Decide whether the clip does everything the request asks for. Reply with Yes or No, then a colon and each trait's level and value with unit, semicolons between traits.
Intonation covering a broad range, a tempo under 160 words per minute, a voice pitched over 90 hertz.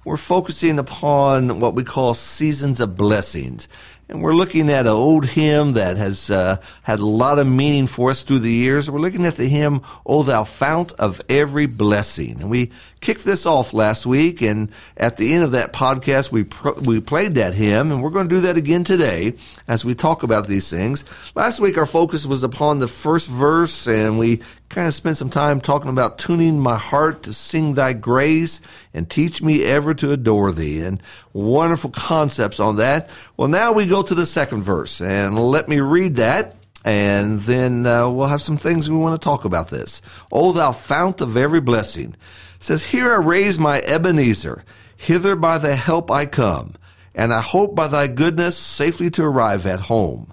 No: wide, 6.1 semitones; average, 200 wpm; low, 135 Hz